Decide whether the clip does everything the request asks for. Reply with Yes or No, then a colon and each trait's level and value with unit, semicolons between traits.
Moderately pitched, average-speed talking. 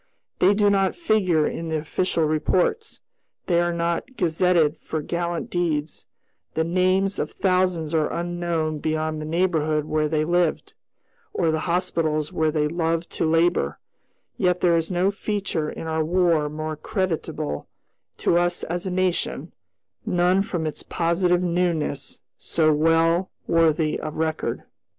Yes: medium, 170 Hz; average, 145 wpm